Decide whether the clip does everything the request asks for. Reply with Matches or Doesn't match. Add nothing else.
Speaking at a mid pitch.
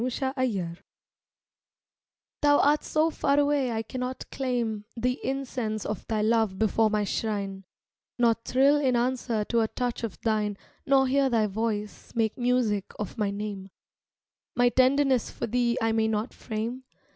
Doesn't match